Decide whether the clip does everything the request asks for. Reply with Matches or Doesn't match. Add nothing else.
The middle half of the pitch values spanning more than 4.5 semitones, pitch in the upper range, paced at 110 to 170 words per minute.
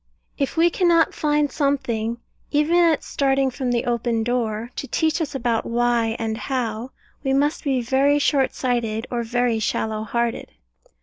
Doesn't match